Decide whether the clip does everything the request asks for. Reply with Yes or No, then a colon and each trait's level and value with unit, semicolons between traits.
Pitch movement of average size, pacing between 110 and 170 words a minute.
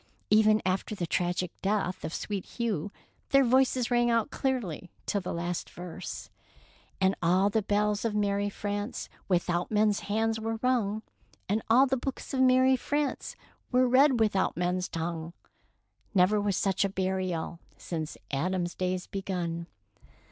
Yes: average, 4.1 semitones; average, 155 wpm